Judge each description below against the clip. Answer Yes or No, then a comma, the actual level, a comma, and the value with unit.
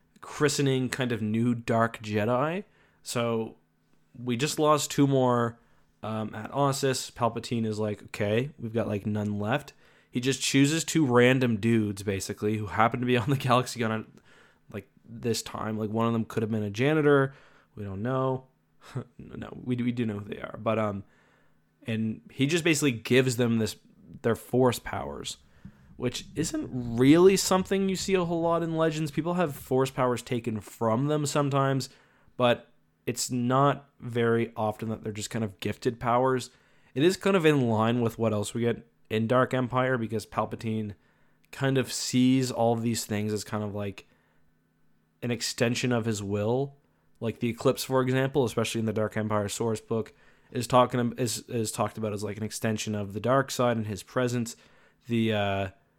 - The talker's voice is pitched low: Yes, low, 120 Hz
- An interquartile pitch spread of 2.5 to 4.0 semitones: Yes, average, 3.4 semitones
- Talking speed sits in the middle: Yes, average, 180 wpm